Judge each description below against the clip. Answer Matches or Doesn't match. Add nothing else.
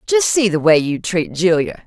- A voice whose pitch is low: Doesn't match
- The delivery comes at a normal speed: Doesn't match